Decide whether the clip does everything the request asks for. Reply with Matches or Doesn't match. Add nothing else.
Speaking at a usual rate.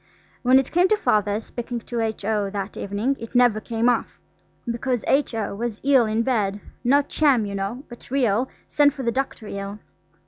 Matches